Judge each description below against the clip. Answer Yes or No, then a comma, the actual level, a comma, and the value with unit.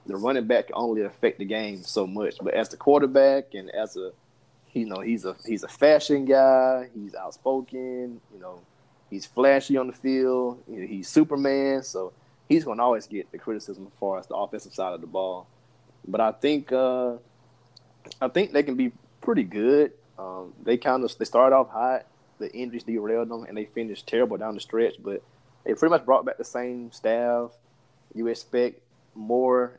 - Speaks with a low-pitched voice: Yes, low, 120 Hz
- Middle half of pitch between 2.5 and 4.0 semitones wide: Yes, average, 3.4 semitones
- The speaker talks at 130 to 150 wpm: No, average, 195 wpm